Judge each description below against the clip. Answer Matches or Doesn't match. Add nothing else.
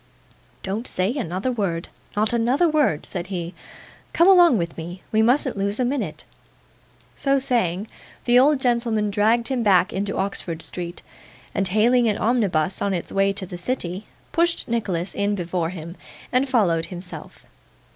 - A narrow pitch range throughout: Doesn't match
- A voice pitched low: Doesn't match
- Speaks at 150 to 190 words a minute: Matches